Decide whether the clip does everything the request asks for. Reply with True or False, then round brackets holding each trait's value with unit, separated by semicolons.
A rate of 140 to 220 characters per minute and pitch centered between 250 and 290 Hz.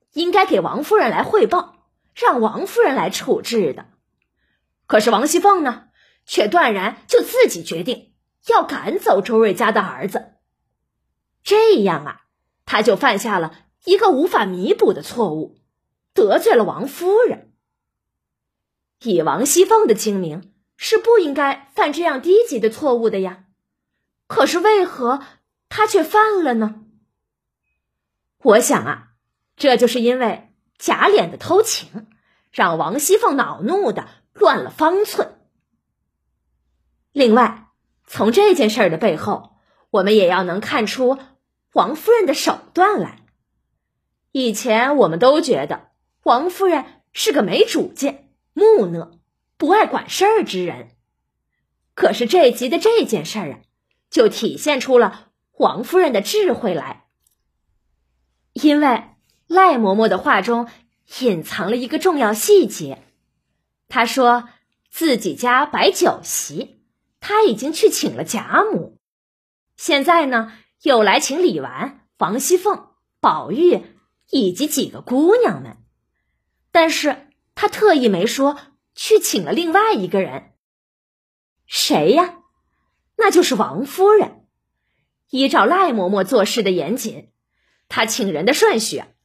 True (190 characters per minute; 280 Hz)